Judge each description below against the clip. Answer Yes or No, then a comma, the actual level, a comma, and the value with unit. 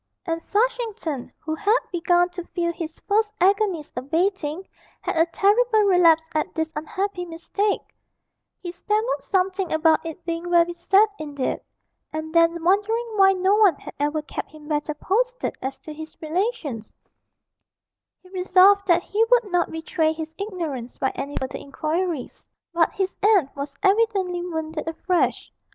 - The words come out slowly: No, average, 150 wpm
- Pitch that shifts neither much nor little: Yes, average, 4.0 semitones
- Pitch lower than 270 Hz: No, very high, 345 Hz